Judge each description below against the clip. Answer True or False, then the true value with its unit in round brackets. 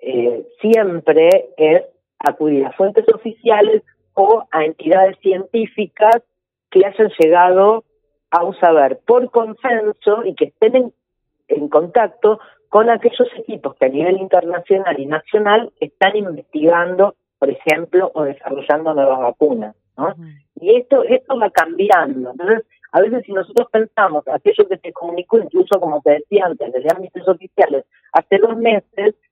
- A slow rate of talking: False (140 wpm)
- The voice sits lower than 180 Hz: False (195 Hz)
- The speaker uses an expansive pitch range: True (6.3 semitones)